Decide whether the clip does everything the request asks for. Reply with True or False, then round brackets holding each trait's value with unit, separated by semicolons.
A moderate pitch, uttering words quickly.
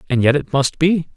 True (150 Hz; 260 wpm)